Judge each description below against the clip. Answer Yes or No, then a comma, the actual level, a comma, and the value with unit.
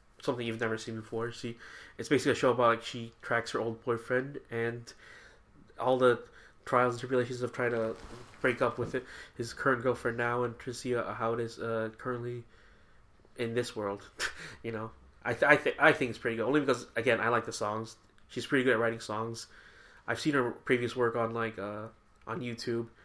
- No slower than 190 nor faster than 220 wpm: Yes, fast, 205 wpm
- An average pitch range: No, narrow, 1.4 semitones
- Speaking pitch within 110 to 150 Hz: Yes, low, 115 Hz